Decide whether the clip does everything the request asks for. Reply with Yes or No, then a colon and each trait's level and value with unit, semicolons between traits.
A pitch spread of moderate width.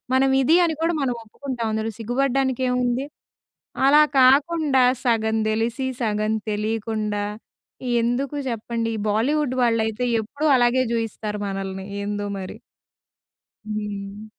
Yes: average, 3.6 semitones